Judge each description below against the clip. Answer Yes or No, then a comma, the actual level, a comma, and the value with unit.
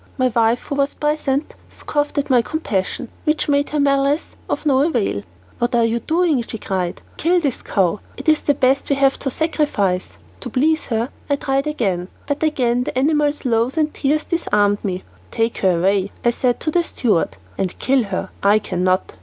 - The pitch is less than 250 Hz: No, very high, 260 Hz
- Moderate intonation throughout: No, wide, 5.8 semitones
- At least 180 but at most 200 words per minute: Yes, average, 190 wpm